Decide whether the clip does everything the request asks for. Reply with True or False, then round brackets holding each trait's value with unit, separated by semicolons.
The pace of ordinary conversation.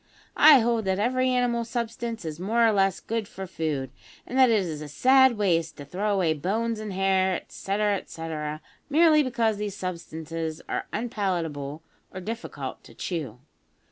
True (165 wpm)